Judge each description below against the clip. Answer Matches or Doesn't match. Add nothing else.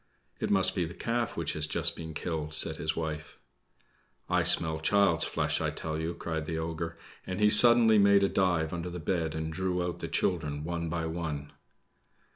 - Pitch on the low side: Matches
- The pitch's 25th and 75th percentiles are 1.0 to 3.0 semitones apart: Matches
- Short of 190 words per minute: Doesn't match